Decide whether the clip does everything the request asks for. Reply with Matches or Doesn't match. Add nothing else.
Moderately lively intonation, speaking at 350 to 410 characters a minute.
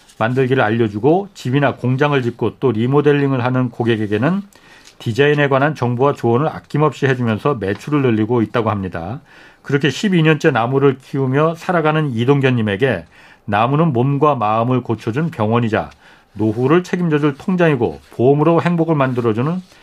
Matches